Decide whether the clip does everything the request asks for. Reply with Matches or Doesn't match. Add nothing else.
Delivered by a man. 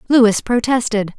Doesn't match